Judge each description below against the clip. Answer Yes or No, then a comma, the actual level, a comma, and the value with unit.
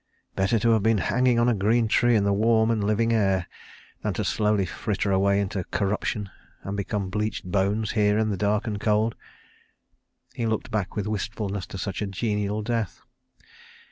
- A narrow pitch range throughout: Yes, narrow, 1.9 semitones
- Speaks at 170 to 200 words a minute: Yes, average, 180 wpm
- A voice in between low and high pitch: No, low, 105 Hz